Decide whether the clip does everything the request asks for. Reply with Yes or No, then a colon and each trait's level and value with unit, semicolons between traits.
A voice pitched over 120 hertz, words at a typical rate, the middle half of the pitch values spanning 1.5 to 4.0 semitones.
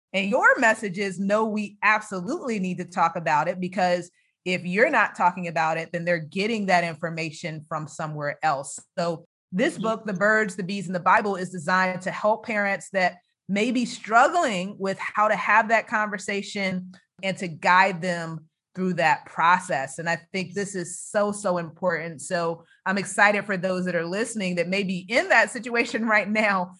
Yes: medium, 185 Hz; average, 185 wpm; average, 2.9 semitones